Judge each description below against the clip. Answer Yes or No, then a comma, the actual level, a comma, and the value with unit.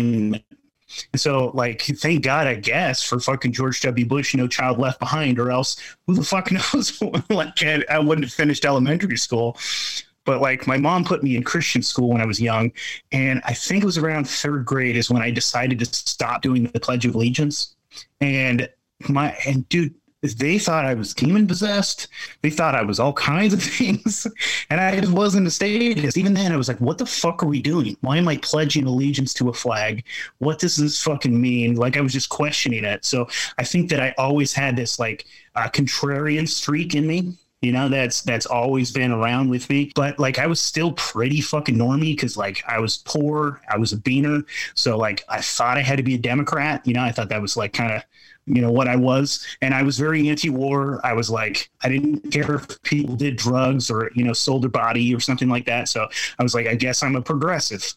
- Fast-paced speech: Yes, fast, 220 wpm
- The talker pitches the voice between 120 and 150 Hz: Yes, low, 135 Hz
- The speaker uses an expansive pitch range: No, average, 3.6 semitones